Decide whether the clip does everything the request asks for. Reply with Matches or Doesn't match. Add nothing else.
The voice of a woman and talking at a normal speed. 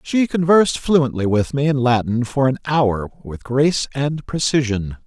Doesn't match